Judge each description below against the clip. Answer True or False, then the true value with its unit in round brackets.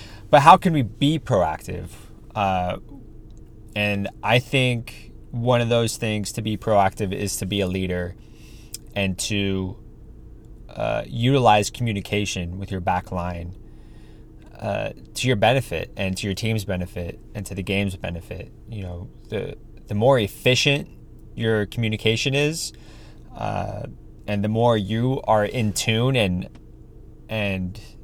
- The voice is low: True (110 Hz)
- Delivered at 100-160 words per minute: True (135 wpm)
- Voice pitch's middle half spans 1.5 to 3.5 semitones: True (2.8 semitones)